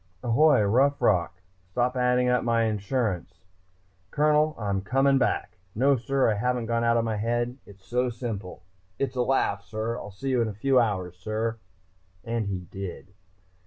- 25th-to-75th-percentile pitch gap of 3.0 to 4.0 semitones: Yes, average, 3.6 semitones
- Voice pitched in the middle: No, low, 115 Hz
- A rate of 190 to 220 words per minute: No, average, 170 wpm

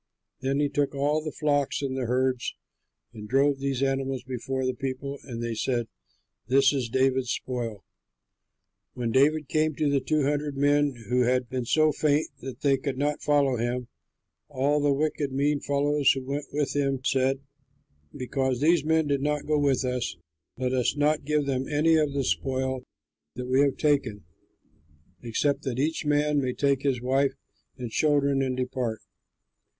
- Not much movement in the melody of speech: Yes, narrow, 2.1 semitones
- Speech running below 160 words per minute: No, average, 170 wpm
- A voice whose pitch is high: No, low, 135 Hz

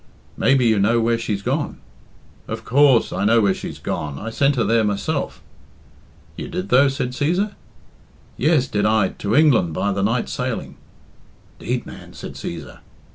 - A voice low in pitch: Yes, low, 115 Hz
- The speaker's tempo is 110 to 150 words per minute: No, average, 165 wpm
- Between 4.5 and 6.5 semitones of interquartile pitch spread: Yes, average, 5.1 semitones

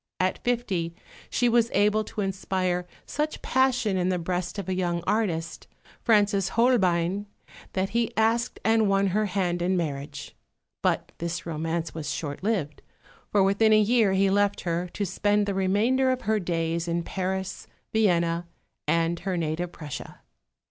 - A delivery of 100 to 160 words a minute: Yes, average, 155 wpm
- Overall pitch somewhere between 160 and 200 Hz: Yes, high, 190 Hz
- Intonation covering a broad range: No, average, 3.8 semitones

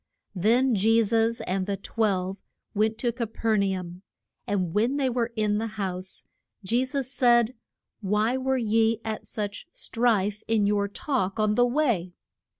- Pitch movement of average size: Yes, average, 3.0 semitones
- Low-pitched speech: No, high, 220 Hz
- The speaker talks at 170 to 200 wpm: No, average, 160 wpm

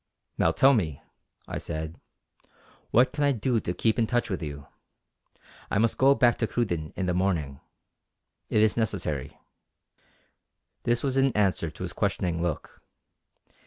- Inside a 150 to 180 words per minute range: Yes, average, 155 wpm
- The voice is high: No, low, 100 Hz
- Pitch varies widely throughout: Yes, wide, 6.3 semitones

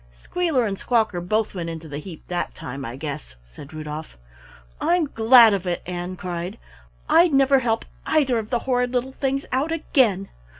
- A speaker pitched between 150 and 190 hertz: No, high, 215 Hz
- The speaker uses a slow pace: No, average, 175 wpm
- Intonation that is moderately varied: No, wide, 7.3 semitones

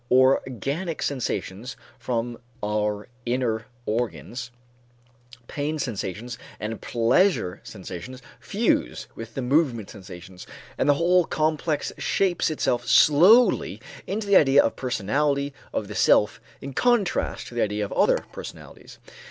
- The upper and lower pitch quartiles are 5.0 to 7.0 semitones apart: Yes, wide, 5.6 semitones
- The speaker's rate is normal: No, slow, 125 wpm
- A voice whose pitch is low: Yes, low, 125 Hz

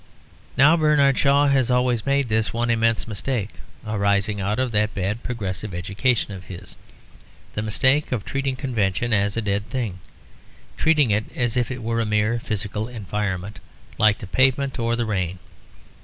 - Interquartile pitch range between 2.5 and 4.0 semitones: Yes, average, 3.7 semitones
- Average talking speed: Yes, average, 165 wpm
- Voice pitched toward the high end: No, low, 115 Hz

